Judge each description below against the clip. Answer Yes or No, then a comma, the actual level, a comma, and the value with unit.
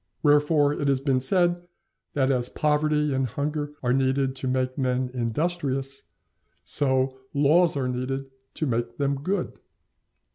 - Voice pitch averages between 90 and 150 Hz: Yes, low, 135 Hz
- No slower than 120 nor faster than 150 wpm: Yes, average, 140 wpm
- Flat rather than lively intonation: Yes, narrow, 2.2 semitones